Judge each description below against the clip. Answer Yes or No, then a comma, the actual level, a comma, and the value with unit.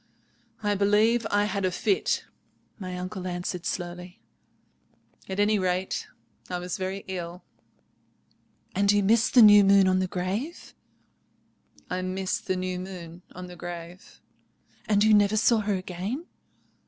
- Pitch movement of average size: No, narrow, 2.3 semitones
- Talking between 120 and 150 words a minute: Yes, average, 140 wpm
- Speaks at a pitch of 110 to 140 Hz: No, high, 190 Hz